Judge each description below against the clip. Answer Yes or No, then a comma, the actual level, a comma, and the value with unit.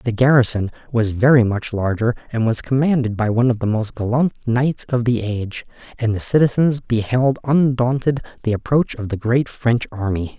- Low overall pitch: Yes, low, 120 Hz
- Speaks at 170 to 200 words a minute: Yes, average, 180 wpm